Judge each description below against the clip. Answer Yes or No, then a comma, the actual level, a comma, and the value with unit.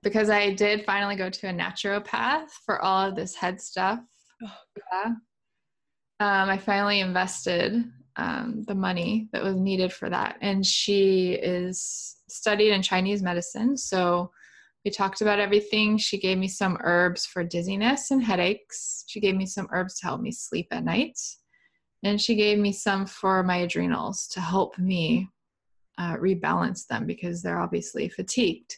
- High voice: Yes, high, 195 Hz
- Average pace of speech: Yes, average, 160 wpm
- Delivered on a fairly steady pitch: Yes, narrow, 2.3 semitones